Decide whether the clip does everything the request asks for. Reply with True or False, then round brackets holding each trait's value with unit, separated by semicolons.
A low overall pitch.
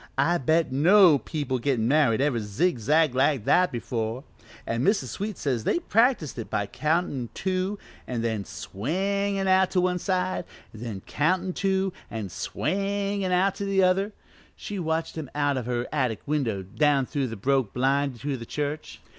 False (150 Hz)